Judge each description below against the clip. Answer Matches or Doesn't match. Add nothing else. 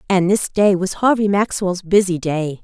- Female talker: Matches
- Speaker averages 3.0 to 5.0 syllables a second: Matches